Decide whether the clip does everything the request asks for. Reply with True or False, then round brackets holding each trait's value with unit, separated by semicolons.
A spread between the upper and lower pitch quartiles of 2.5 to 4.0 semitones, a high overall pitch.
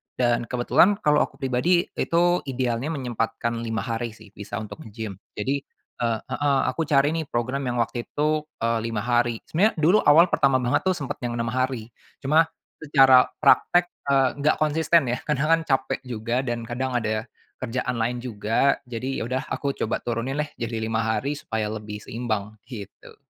False (3.7 semitones; 125 Hz)